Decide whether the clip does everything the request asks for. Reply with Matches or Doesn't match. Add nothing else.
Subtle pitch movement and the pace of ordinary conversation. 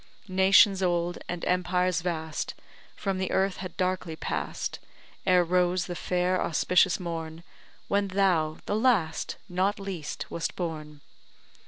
Doesn't match